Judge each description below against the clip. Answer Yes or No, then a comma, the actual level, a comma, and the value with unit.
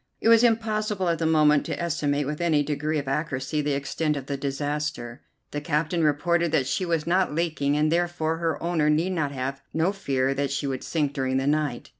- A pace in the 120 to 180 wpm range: No, fast, 205 wpm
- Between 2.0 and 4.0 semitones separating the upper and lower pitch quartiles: Yes, average, 3.1 semitones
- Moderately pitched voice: Yes, medium, 150 Hz